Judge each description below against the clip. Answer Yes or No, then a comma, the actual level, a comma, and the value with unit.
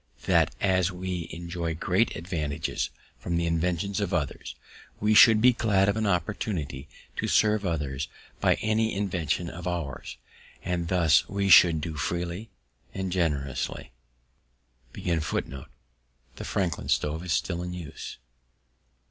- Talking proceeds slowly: Yes, slow, 130 wpm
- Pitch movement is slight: No, average, 3.9 semitones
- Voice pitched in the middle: No, very low, 85 Hz